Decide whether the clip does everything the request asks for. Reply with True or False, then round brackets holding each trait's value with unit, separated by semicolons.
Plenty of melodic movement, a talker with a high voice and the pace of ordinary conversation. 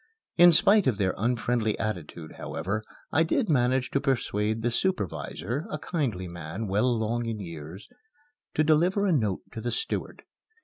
False (7.2 semitones; 115 Hz; 160 wpm)